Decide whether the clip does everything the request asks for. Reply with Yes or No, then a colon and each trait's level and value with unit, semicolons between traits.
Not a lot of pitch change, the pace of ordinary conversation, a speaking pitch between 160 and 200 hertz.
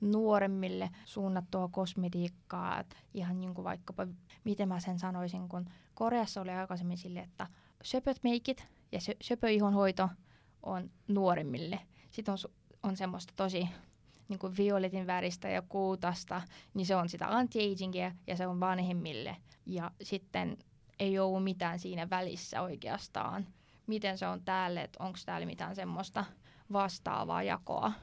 Yes: narrow, 1.7 semitones; average, 135 wpm; medium, 185 Hz